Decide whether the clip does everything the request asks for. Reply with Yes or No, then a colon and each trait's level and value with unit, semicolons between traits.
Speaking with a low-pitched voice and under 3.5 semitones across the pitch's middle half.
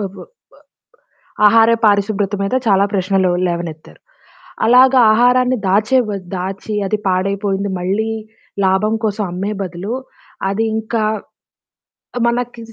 No: high, 205 Hz; average, 2.7 semitones